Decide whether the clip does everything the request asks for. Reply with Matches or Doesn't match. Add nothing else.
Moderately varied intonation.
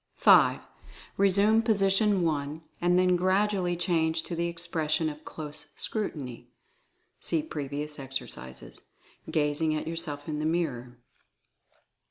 Matches